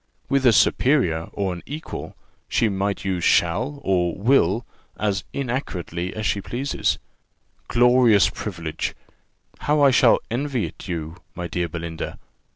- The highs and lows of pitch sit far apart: Yes, wide, 6.4 semitones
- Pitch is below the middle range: Yes, low, 100 Hz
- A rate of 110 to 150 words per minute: Yes, slow, 135 wpm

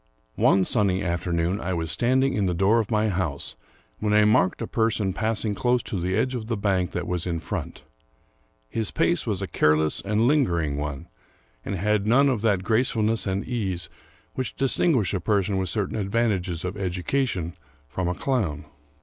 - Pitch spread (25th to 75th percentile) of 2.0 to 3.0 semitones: No, average, 4.1 semitones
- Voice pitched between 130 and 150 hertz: No, low, 100 Hz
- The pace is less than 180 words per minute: No, average, 185 wpm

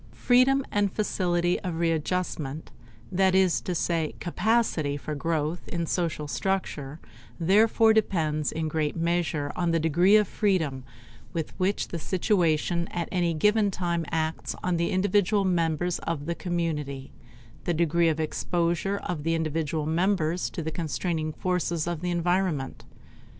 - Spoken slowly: No, average, 145 wpm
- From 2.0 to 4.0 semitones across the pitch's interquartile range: Yes, average, 2.7 semitones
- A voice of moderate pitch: Yes, medium, 170 Hz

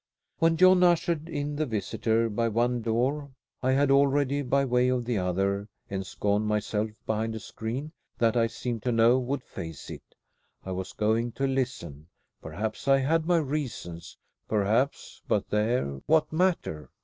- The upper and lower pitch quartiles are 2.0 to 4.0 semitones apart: No, average, 4.9 semitones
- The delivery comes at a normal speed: Yes, average, 160 wpm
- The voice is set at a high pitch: No, low, 120 Hz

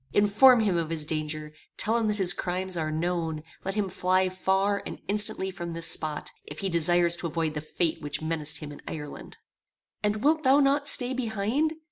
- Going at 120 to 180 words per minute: No, average, 195 wpm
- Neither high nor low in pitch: Yes, medium, 180 Hz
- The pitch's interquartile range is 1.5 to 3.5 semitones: No, average, 4.7 semitones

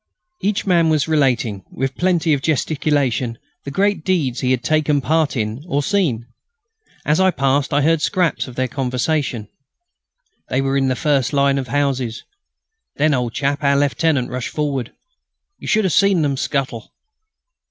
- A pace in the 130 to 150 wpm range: No, average, 165 wpm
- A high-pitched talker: No, medium, 140 Hz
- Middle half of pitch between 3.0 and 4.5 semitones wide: Yes, average, 3.4 semitones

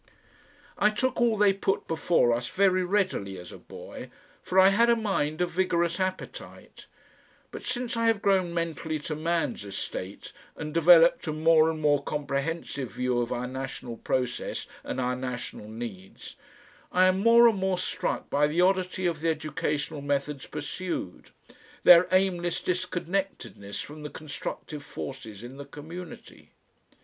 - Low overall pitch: No, medium, 165 Hz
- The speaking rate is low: No, average, 155 wpm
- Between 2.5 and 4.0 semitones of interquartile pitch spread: No, average, 5.2 semitones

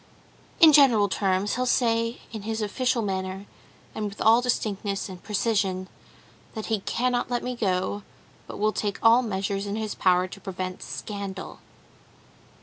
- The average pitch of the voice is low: No, high, 210 Hz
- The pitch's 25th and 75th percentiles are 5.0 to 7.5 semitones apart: No, average, 3.1 semitones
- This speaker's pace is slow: No, average, 150 wpm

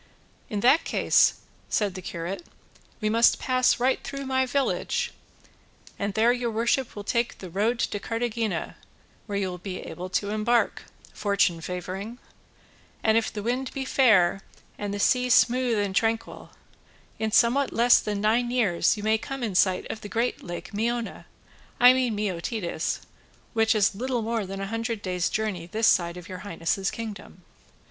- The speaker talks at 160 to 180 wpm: Yes, average, 170 wpm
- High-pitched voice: Yes, high, 220 Hz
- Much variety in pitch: No, average, 3.6 semitones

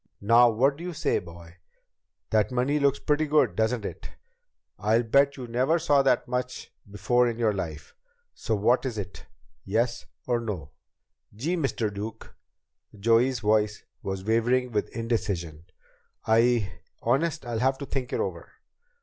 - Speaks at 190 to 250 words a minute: No, average, 150 wpm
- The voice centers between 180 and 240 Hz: No, low, 115 Hz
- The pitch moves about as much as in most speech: Yes, average, 3.8 semitones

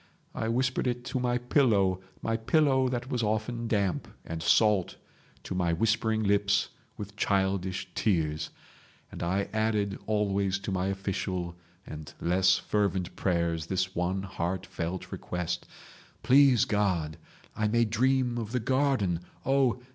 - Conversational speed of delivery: No, slow, 130 wpm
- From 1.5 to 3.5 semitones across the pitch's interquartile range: No, average, 4.2 semitones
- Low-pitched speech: Yes, low, 100 Hz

